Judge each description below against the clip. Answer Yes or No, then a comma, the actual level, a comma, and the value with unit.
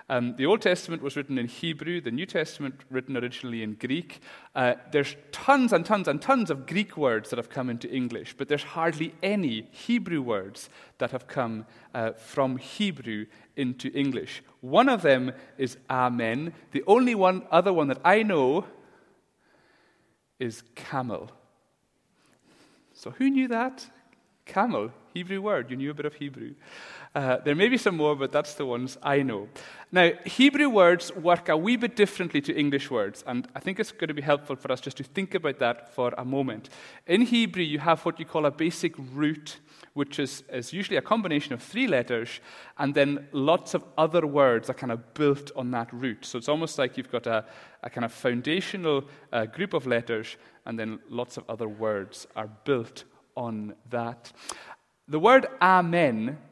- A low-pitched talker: No, medium, 145 Hz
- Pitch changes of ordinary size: No, wide, 5.7 semitones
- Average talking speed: Yes, average, 185 wpm